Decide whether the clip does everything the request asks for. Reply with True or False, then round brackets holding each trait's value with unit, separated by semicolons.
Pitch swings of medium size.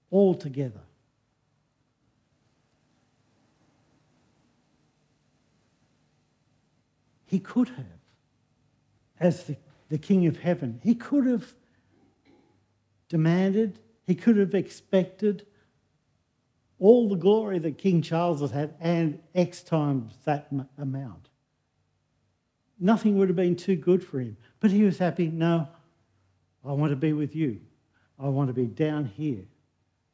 False (5.7 semitones)